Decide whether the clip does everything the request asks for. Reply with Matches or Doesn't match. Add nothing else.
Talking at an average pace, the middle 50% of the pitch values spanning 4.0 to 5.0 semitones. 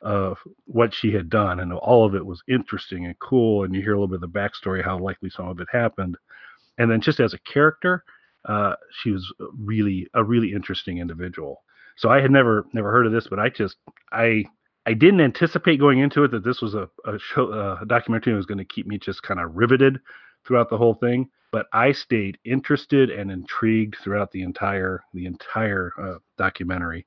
Doesn't match